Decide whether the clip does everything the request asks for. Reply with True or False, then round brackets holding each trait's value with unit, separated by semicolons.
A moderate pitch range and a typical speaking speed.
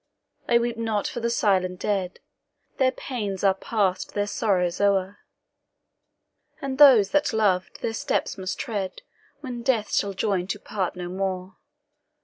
True (3.7 semitones; 145 wpm)